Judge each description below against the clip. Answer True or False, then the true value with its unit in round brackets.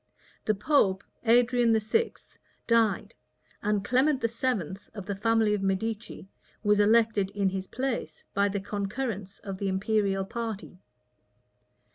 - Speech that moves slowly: True (125 wpm)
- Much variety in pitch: False (3.0 semitones)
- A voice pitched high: True (210 Hz)